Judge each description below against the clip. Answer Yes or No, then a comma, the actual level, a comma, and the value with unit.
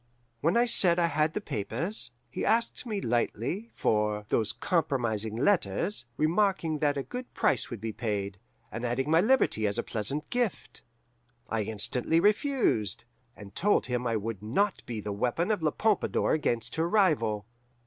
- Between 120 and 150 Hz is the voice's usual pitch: Yes, medium, 140 Hz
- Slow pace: No, average, 165 wpm